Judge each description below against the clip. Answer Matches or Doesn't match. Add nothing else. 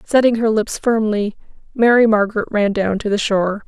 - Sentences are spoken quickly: Doesn't match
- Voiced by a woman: Matches